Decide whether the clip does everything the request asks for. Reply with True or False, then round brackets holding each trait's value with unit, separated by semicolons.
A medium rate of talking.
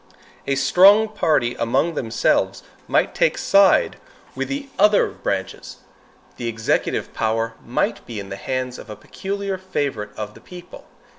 True (145 wpm)